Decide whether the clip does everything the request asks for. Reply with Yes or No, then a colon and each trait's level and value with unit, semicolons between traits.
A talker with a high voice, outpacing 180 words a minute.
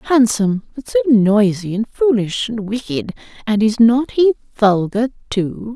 No: high, 225 Hz; average, 145 wpm